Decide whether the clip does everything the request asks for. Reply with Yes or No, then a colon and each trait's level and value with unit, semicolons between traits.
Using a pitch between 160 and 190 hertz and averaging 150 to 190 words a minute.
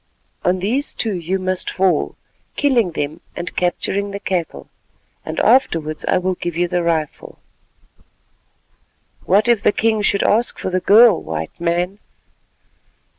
No: medium, 185 Hz; average, 140 wpm